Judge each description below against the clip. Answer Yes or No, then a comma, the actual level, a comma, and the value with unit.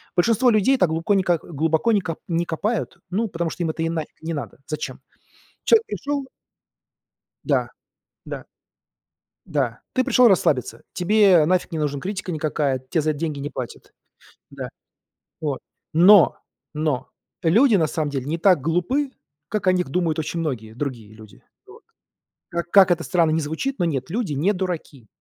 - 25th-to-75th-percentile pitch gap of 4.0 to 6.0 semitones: Yes, average, 4.4 semitones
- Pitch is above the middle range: No, medium, 165 Hz